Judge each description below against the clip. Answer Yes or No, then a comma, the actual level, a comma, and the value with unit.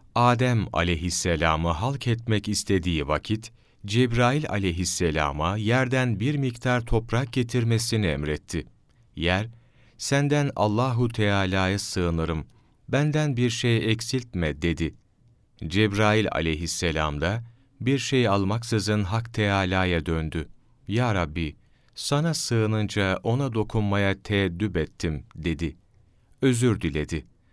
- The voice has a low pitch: Yes, low, 105 Hz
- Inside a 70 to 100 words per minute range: Yes, slow, 95 wpm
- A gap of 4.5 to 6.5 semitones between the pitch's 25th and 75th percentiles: Yes, wide, 5.6 semitones